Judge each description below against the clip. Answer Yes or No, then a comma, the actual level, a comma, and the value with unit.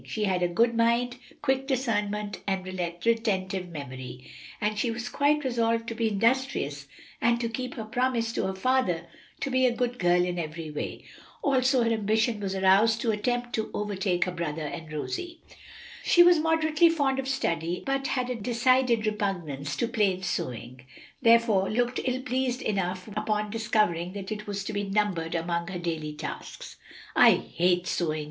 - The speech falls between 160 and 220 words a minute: Yes, average, 170 wpm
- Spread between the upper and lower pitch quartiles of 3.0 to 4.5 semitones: No, wide, 5.5 semitones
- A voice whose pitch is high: Yes, high, 215 Hz